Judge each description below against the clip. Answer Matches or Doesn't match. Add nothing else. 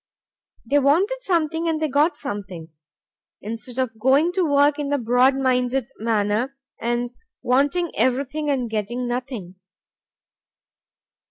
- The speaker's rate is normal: Doesn't match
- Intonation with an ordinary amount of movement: Matches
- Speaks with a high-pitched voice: Matches